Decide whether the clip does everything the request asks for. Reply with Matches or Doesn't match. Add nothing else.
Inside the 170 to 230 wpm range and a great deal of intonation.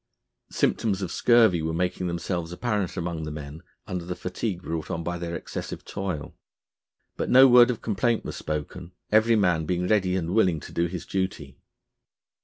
Doesn't match